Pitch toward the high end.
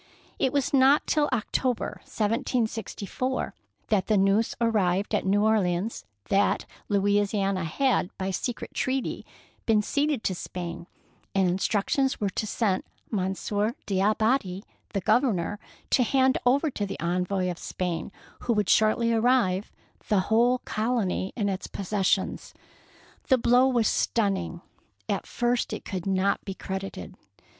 Yes: high, 210 Hz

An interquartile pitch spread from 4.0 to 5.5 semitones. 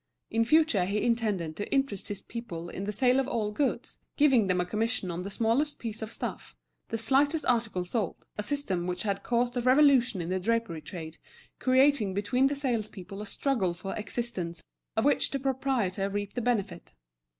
Yes: average, 5.0 semitones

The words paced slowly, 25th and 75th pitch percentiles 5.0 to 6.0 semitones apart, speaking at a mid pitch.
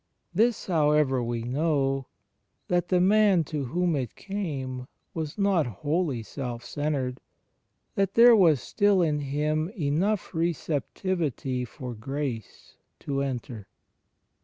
Yes: slow, 120 wpm; average, 5.3 semitones; medium, 150 Hz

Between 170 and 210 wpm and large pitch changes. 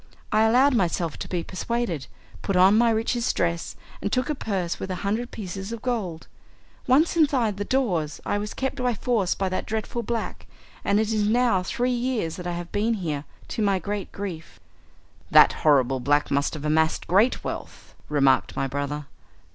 Yes: average, 185 wpm; wide, 5.7 semitones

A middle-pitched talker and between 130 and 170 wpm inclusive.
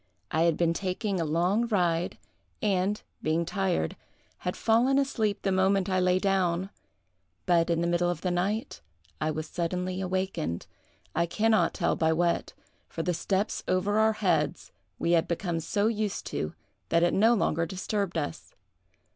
Yes: medium, 180 Hz; average, 165 wpm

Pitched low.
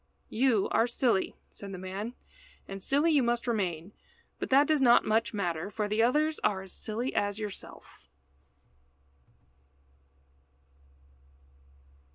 No: high, 220 Hz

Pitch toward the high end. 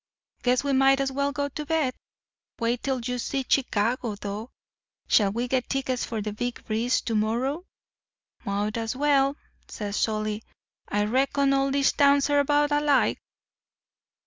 Yes: very high, 255 Hz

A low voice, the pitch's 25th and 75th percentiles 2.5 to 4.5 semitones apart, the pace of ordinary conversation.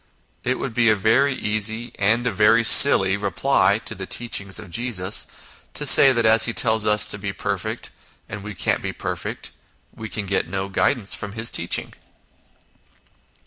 Yes: low, 110 Hz; average, 3.0 semitones; average, 175 wpm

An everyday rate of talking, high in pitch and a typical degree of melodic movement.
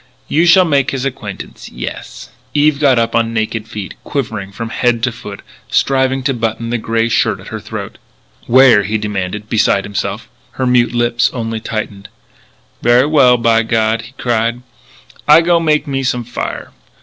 No: average, 170 wpm; low, 115 Hz; average, 3.1 semitones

